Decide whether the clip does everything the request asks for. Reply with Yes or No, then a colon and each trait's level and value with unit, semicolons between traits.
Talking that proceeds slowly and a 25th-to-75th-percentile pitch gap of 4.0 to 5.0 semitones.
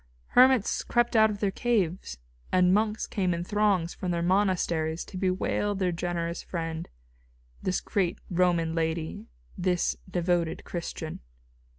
No: slow, 130 wpm; average, 3.1 semitones